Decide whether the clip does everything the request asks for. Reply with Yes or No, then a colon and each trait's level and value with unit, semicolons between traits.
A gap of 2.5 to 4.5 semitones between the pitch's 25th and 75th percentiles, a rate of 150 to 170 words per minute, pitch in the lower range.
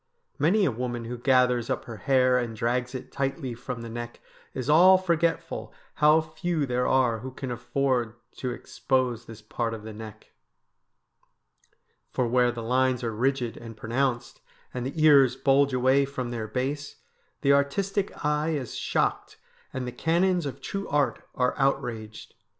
Yes: average, 3.0 semitones; average, 160 wpm; low, 130 Hz